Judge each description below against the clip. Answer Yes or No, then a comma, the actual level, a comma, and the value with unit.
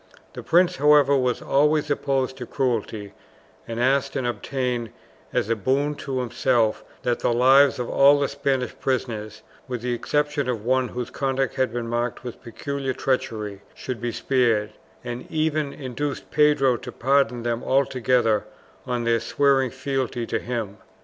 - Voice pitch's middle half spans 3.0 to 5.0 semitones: No, narrow, 2.6 semitones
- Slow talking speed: No, average, 155 wpm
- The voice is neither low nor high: No, low, 130 Hz